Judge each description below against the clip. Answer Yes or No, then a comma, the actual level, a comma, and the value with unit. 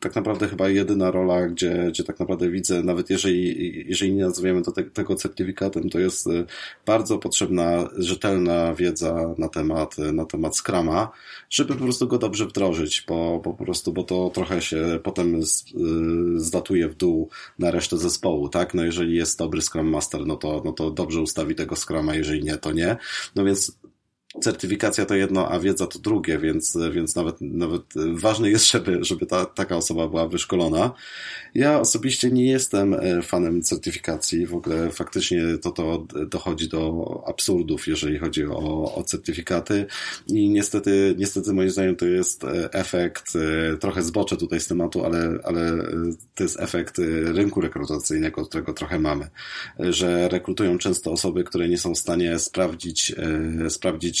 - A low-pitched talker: Yes, very low, 85 Hz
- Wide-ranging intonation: No, narrow, 2.4 semitones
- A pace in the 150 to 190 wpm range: Yes, fast, 160 wpm